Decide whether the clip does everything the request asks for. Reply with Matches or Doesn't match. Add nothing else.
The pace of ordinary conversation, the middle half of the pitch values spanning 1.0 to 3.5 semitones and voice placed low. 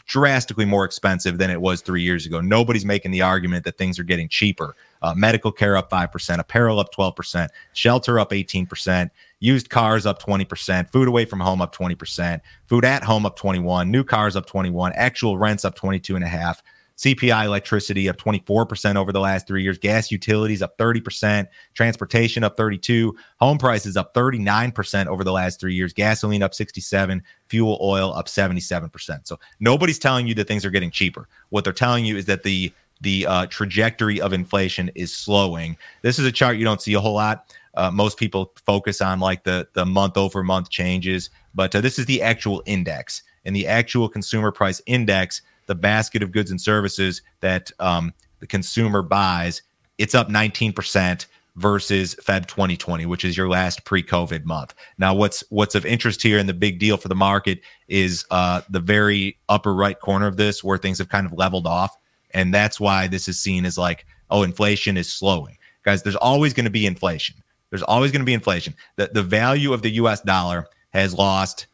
Matches